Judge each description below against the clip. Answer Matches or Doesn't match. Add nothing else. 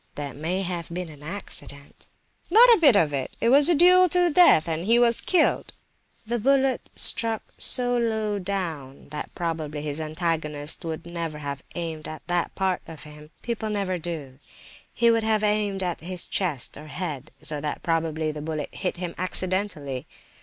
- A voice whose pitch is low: Doesn't match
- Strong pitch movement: Matches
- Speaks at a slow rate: Doesn't match